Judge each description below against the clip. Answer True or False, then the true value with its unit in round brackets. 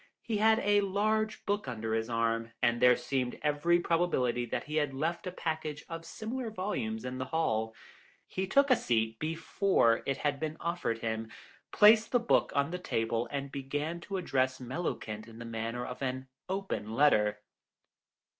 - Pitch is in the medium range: True (145 Hz)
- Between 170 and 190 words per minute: True (175 wpm)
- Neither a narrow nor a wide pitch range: False (7.7 semitones)